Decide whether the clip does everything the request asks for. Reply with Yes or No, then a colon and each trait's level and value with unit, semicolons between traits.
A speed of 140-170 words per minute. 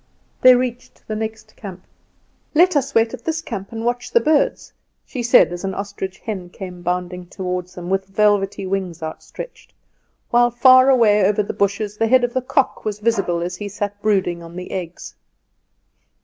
No: average, 180 wpm